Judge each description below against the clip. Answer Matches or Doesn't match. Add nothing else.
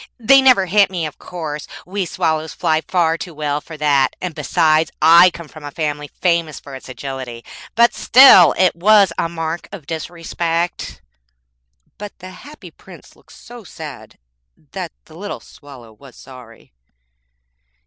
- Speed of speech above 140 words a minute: Matches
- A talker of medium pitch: Matches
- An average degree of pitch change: Matches